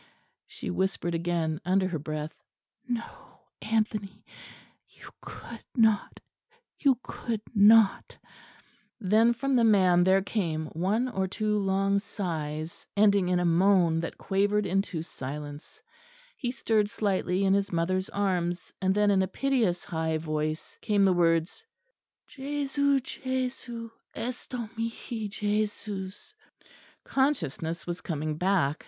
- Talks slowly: Yes, slow, 125 wpm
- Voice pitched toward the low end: No, high, 195 Hz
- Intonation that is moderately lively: Yes, average, 4.4 semitones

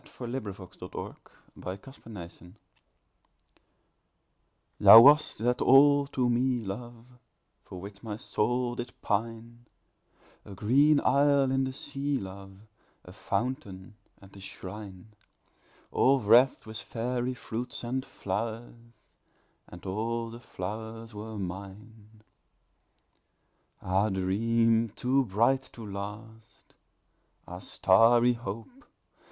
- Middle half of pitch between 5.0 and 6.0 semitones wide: No, average, 3.5 semitones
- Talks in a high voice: No, low, 115 Hz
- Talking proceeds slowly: Yes, slow, 110 wpm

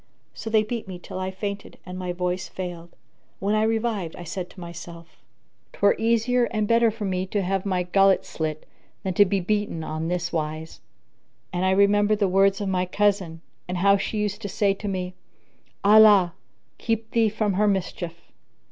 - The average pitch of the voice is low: No, high, 195 Hz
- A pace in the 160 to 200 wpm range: Yes, average, 190 wpm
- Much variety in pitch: No, average, 2.7 semitones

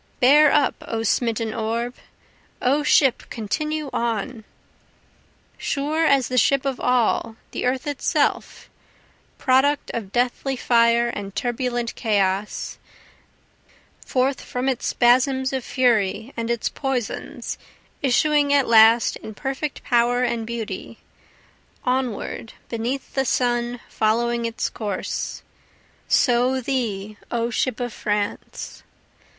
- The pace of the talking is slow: Yes, slow, 110 wpm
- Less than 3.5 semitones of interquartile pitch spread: Yes, narrow, 2.6 semitones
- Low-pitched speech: No, high, 245 Hz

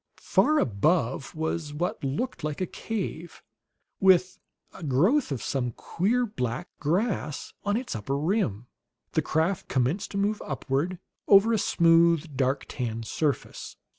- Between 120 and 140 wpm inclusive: Yes, slow, 135 wpm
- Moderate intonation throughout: No, wide, 6.2 semitones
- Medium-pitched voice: Yes, medium, 160 Hz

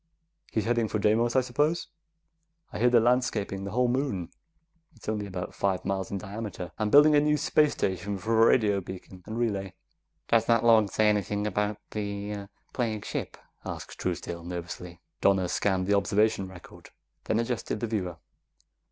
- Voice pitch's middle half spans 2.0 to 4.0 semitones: Yes, average, 3.2 semitones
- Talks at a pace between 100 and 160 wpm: No, average, 170 wpm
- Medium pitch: No, low, 105 Hz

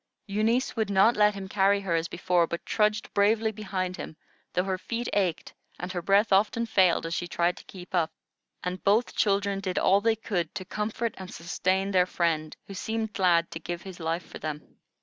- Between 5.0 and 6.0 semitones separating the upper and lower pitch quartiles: No, average, 3.0 semitones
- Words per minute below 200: No, fast, 205 wpm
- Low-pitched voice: No, high, 190 Hz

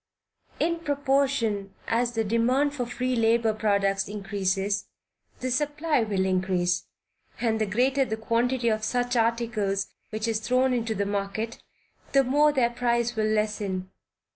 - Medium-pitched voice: No, high, 230 Hz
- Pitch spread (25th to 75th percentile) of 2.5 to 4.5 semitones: Yes, average, 3.5 semitones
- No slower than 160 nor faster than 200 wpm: No, average, 140 wpm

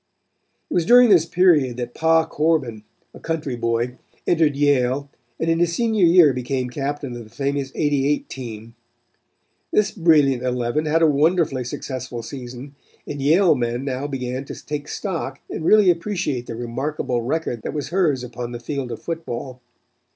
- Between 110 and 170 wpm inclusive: Yes, average, 165 wpm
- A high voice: No, medium, 140 Hz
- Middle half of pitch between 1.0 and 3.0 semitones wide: No, average, 4.7 semitones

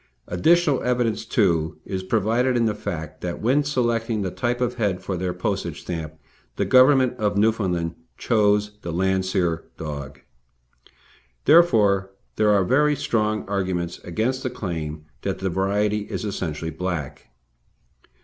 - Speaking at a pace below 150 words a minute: Yes, average, 140 wpm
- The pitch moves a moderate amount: Yes, average, 5.0 semitones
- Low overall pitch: Yes, low, 100 Hz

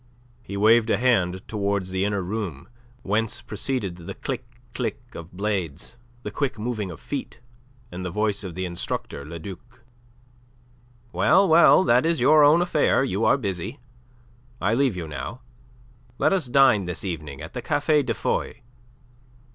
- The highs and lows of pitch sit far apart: Yes, wide, 5.7 semitones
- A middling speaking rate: Yes, average, 160 wpm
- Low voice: Yes, low, 105 Hz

